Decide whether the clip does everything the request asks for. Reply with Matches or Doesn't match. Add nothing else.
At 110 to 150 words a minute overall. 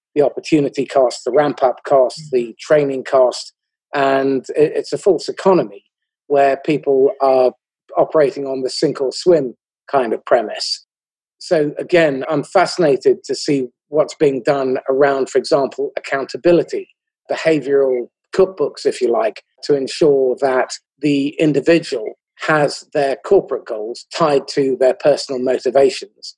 Matches